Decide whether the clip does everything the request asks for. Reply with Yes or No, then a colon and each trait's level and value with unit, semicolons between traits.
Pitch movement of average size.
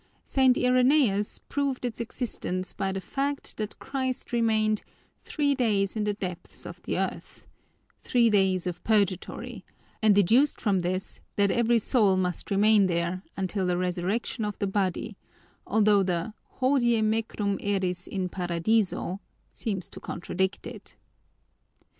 Yes: average, 3.8 semitones